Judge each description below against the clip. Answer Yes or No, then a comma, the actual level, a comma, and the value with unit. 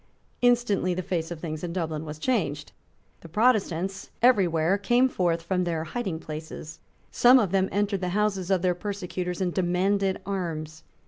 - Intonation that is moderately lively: Yes, average, 3.3 semitones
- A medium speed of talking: Yes, average, 170 wpm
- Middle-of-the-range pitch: Yes, medium, 180 Hz